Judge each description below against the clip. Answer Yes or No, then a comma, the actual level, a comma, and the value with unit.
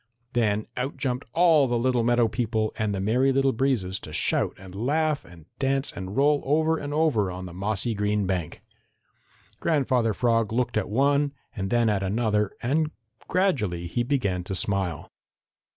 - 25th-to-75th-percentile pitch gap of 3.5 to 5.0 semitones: No, wide, 5.4 semitones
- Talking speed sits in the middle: Yes, average, 170 wpm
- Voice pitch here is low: Yes, low, 115 Hz